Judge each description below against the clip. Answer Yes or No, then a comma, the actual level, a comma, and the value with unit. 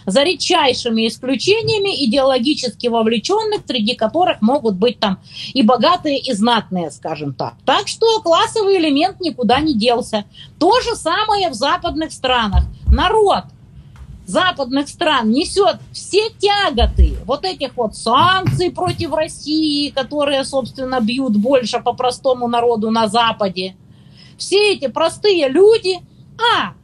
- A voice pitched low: No, very high, 275 Hz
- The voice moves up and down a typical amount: No, wide, 7.0 semitones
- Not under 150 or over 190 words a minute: No, average, 125 wpm